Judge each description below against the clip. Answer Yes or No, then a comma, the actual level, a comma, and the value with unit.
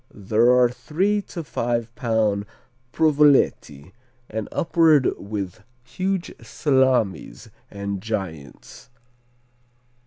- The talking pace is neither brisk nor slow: No, slow, 85 wpm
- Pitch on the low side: Yes, low, 115 Hz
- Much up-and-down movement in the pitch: Yes, wide, 6.8 semitones